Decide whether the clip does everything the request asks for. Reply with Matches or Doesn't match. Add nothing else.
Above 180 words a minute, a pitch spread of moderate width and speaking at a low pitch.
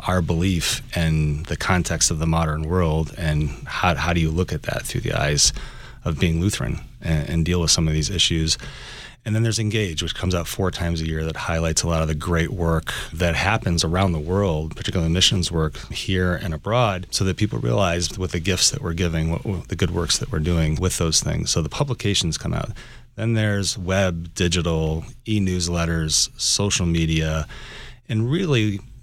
Matches